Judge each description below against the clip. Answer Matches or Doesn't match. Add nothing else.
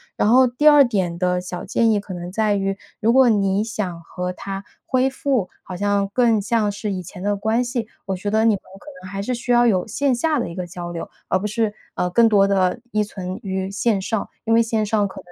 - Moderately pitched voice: Doesn't match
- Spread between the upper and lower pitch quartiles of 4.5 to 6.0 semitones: Doesn't match